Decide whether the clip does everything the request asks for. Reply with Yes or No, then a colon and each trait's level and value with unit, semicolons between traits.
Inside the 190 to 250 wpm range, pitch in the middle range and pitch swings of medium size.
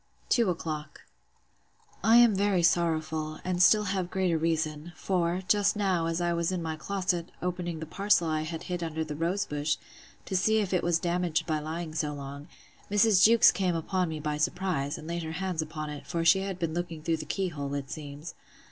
Yes: fast, 205 wpm; medium, 170 Hz; average, 3.0 semitones